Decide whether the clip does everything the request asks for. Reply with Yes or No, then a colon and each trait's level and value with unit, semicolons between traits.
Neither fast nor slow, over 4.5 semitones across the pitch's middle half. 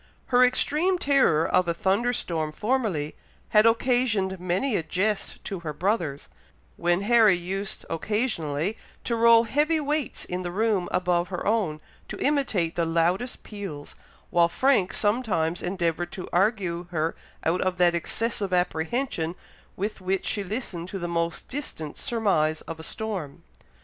Yes: average, 150 wpm; average, 5.1 semitones